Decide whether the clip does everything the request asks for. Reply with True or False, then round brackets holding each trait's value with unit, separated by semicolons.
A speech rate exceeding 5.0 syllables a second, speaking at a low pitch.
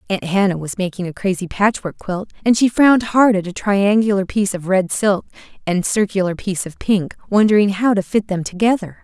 False (5.5 syllables/s; 200 Hz)